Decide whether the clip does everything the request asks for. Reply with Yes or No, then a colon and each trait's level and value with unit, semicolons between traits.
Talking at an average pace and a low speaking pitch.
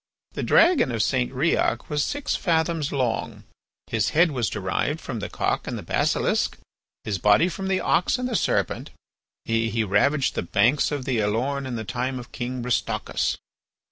Yes: average, 170 wpm; low, 130 Hz